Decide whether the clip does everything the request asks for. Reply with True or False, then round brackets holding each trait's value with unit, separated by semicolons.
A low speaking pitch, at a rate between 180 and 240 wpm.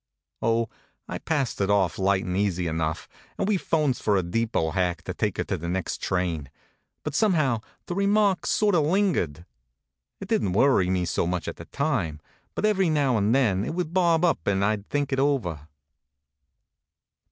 True (110 Hz; 190 wpm)